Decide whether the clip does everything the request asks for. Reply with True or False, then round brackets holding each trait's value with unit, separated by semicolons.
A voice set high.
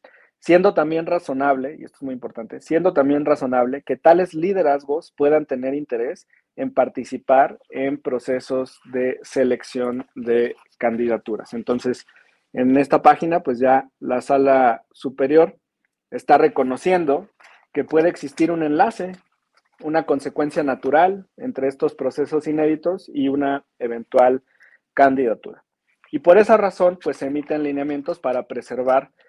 False (140 Hz)